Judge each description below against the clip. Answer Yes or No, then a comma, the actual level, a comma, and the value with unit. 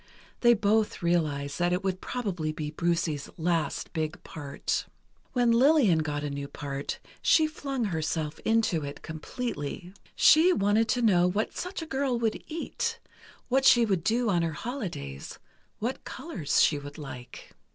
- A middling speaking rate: Yes, average, 155 wpm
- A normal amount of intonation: No, wide, 7.6 semitones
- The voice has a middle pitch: Yes, medium, 180 Hz